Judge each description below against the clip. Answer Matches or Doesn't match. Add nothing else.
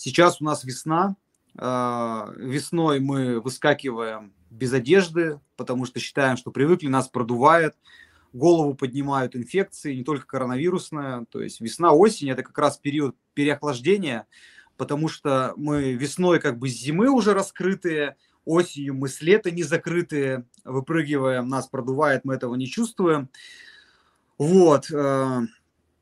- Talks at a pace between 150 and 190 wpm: Doesn't match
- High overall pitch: Doesn't match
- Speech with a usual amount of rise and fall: Matches